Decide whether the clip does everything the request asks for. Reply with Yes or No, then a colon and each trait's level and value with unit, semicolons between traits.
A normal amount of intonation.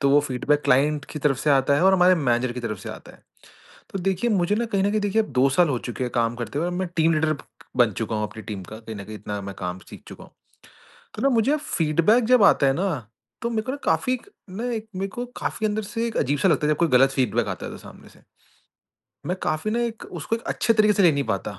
No: wide, 9.0 semitones